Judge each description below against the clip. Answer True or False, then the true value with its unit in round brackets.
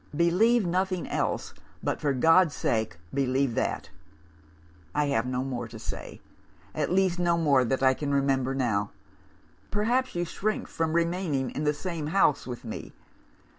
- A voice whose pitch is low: False (150 Hz)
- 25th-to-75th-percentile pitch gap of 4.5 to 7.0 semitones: True (5.1 semitones)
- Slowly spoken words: False (155 wpm)